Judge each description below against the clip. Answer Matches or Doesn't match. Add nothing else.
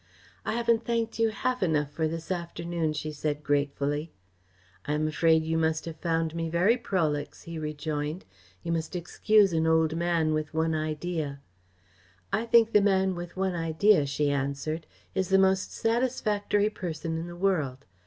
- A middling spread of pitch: Matches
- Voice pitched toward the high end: Doesn't match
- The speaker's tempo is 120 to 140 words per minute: Doesn't match